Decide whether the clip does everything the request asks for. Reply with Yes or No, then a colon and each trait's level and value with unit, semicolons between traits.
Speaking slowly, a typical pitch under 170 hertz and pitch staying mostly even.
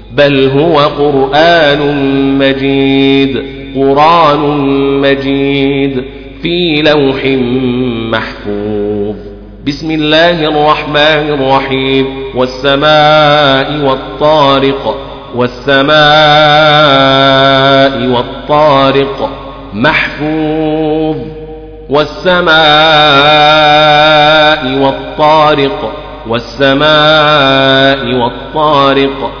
Yes: slow, 45 wpm; medium, 140 Hz; narrow, 1.9 semitones